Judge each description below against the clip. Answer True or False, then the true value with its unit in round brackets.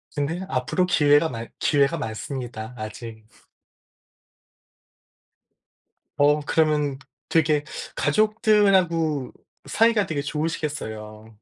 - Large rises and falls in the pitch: False (5.0 semitones)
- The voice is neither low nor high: True (145 Hz)